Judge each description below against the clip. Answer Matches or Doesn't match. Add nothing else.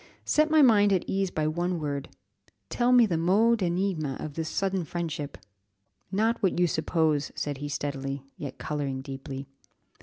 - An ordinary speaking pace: Matches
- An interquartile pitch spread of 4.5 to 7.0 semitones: Matches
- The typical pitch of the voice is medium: Matches